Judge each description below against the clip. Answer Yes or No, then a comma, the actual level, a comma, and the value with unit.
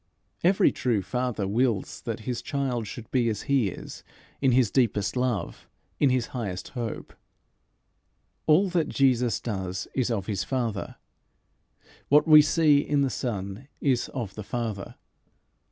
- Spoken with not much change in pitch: No, average, 4.3 semitones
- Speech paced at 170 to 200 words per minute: No, average, 145 wpm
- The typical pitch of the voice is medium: No, low, 120 Hz